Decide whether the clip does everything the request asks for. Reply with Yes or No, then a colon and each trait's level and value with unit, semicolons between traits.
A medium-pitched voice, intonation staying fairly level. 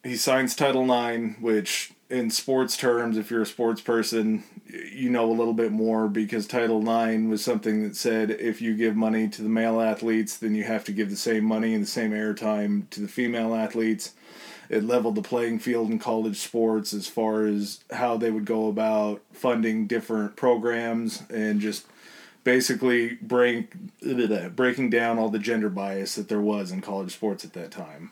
No: low, 110 Hz; narrow, 1.5 semitones